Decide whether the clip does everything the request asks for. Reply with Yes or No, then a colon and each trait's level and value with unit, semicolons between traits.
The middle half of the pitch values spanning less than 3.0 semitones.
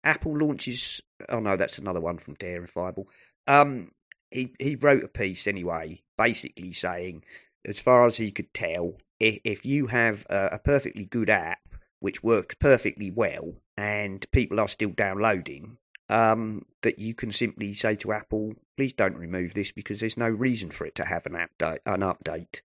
No: average, 3.8 semitones